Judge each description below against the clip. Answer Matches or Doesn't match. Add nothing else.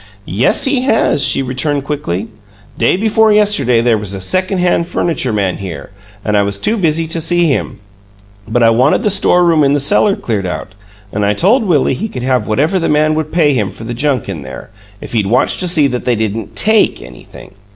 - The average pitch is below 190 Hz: Matches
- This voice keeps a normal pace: Doesn't match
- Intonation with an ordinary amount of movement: Doesn't match